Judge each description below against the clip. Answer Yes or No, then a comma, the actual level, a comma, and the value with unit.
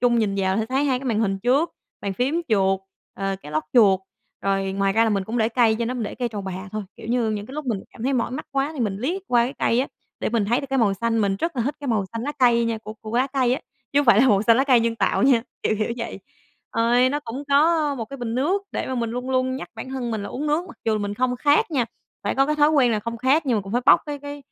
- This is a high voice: Yes, high, 235 Hz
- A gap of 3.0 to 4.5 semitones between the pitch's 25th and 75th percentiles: Yes, average, 3.8 semitones